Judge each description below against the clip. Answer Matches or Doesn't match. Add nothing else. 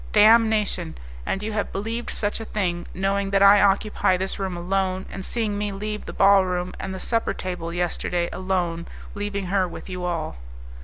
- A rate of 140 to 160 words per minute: Doesn't match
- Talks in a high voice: Matches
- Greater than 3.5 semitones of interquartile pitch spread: Doesn't match